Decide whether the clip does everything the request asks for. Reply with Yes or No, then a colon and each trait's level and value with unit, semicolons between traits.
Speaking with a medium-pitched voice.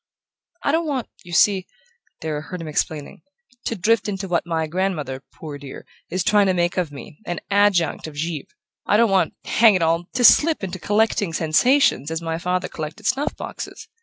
Yes: medium, 180 Hz